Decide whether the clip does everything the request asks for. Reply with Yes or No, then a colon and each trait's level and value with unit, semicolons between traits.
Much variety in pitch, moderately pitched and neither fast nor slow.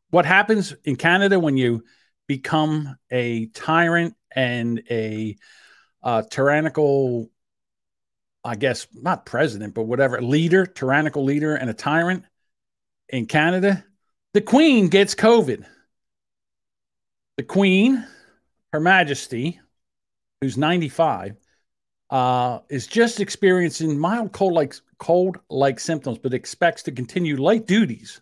No: wide, 6.5 semitones; medium, 155 Hz; slow, 110 wpm